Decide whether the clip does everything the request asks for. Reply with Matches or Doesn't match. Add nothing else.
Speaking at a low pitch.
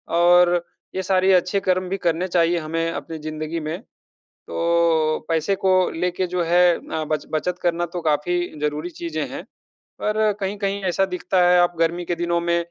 Doesn't match